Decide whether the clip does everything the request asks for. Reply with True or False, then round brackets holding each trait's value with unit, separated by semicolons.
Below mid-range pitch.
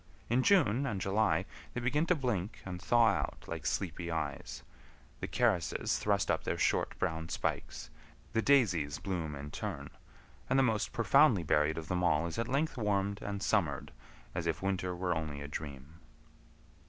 True (95 Hz)